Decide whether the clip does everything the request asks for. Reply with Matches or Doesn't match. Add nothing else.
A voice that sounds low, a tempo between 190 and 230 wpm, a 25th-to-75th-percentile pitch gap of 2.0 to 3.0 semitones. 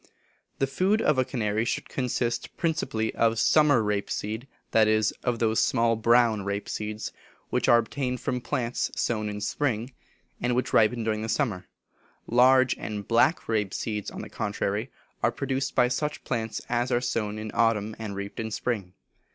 Doesn't match